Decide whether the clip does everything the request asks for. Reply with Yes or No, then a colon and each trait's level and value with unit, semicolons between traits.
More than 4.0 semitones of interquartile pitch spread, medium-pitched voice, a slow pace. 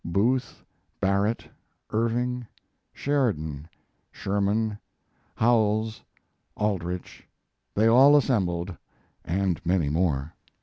No: average, 4.8 semitones; low, 105 Hz; slow, 75 wpm